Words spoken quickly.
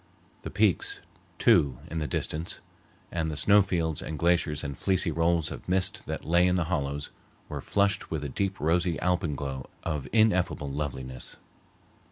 No: average, 160 wpm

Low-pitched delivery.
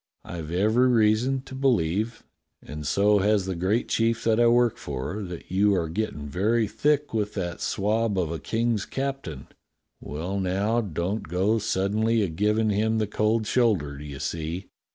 Yes: low, 105 Hz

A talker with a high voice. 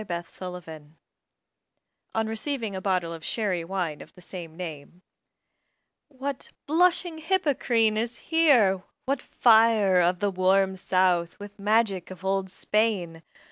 Yes: high, 195 Hz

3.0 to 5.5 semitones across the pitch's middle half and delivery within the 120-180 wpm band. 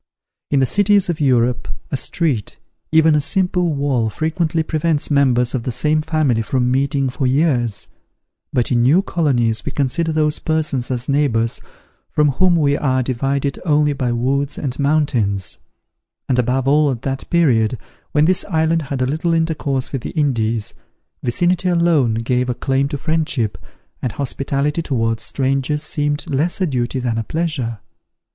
Yes: average, 3.9 semitones; average, 160 wpm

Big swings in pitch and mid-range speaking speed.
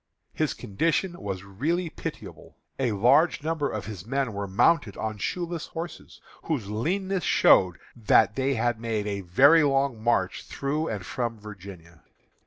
Yes: wide, 7.3 semitones; average, 150 wpm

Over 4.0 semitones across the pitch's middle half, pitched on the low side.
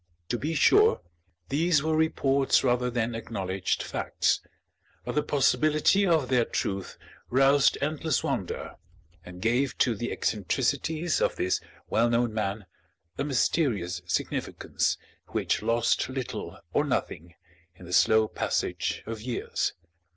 Yes: average, 5.1 semitones; low, 125 Hz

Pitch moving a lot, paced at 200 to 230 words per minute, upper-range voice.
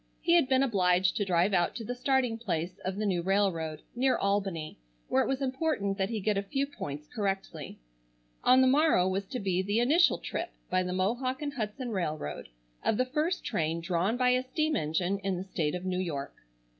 Yes: wide, 6.0 semitones; fast, 205 wpm; high, 200 Hz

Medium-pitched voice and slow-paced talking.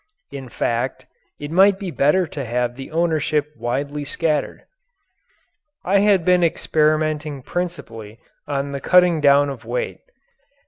Yes: medium, 150 Hz; slow, 130 wpm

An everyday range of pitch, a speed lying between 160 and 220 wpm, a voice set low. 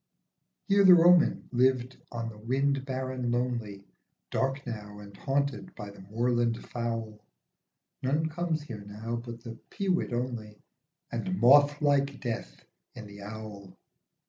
No: average, 4.4 semitones; slow, 135 wpm; low, 120 Hz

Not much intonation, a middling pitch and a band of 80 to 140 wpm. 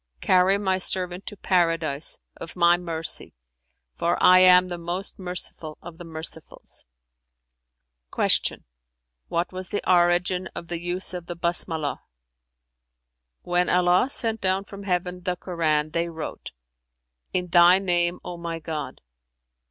Yes: narrow, 1.5 semitones; medium, 175 Hz; slow, 135 wpm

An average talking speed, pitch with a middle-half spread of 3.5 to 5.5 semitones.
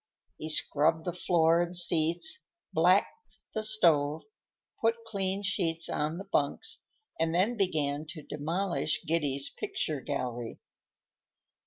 No: slow, 120 wpm; average, 4.2 semitones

